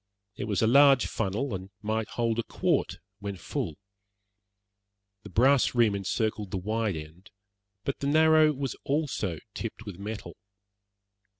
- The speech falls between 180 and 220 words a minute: No, average, 140 wpm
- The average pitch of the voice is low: Yes, low, 110 Hz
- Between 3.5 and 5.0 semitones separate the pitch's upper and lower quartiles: No, wide, 5.4 semitones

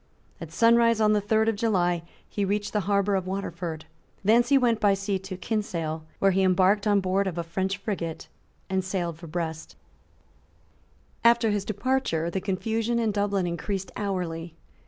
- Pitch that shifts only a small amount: No, average, 3.2 semitones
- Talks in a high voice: Yes, high, 195 Hz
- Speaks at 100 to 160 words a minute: No, average, 170 wpm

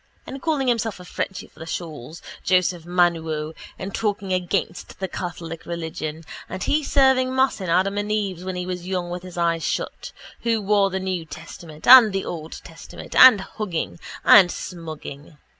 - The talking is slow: No, average, 175 wpm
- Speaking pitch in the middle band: Yes, medium, 180 Hz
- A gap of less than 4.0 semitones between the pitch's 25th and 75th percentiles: Yes, average, 3.6 semitones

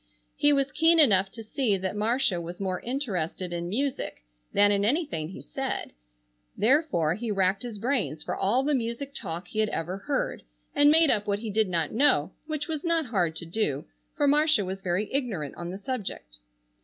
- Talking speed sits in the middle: Yes, average, 190 wpm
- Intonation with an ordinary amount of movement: No, wide, 7.2 semitones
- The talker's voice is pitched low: No, high, 210 Hz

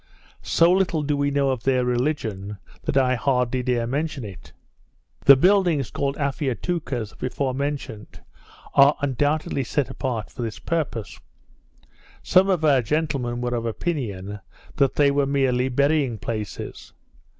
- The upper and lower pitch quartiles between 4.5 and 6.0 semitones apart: No, average, 3.3 semitones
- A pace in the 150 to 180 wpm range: No, average, 140 wpm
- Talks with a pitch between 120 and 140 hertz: Yes, low, 135 Hz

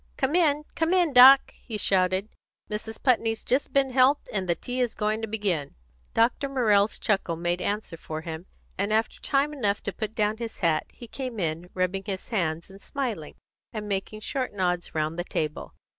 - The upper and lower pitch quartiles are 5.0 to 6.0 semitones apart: Yes, wide, 5.5 semitones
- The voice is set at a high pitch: Yes, high, 210 Hz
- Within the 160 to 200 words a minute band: Yes, average, 190 wpm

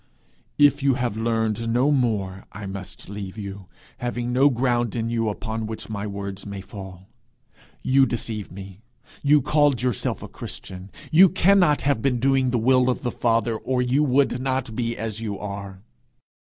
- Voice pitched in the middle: No, low, 115 Hz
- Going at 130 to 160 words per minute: No, average, 170 wpm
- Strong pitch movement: No, average, 4.3 semitones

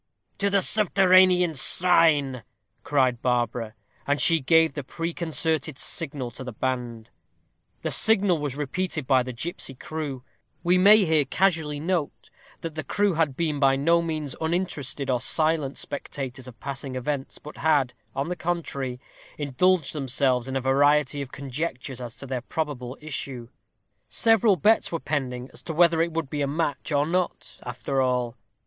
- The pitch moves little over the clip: No, average, 4.2 semitones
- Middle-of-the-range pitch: Yes, medium, 145 Hz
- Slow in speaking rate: No, average, 160 wpm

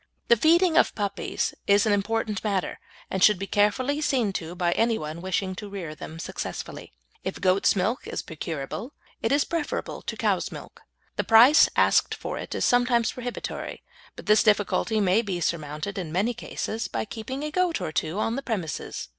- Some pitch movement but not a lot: Yes, average, 4.7 semitones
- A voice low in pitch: No, high, 210 Hz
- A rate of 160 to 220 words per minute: Yes, average, 180 wpm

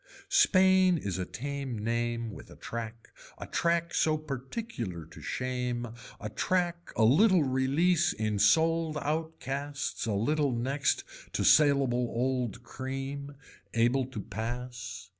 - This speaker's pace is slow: Yes, slow, 130 wpm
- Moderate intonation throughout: Yes, average, 4.8 semitones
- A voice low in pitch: Yes, low, 130 Hz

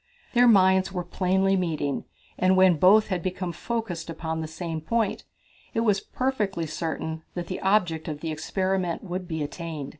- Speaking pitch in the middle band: Yes, medium, 180 Hz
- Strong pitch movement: No, average, 3.1 semitones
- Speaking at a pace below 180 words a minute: Yes, average, 170 wpm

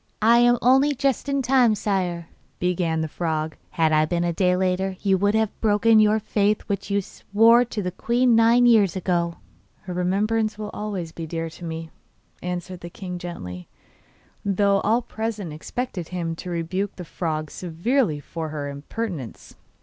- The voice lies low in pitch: No, high, 190 Hz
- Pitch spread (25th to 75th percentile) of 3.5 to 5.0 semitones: Yes, average, 4.6 semitones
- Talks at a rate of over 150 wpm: Yes, average, 170 wpm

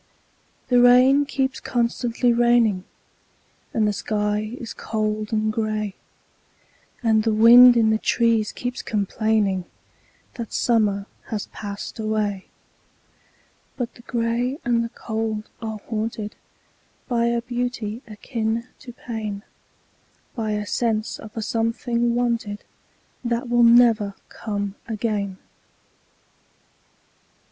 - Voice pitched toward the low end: No, high, 225 Hz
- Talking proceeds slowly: Yes, slow, 95 wpm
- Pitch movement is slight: Yes, narrow, 2.0 semitones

